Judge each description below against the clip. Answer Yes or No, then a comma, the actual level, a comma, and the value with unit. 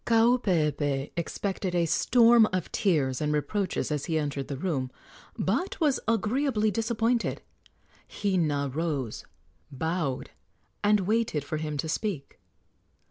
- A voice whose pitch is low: No, medium, 170 Hz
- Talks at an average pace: No, slow, 120 wpm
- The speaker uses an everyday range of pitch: No, wide, 6.7 semitones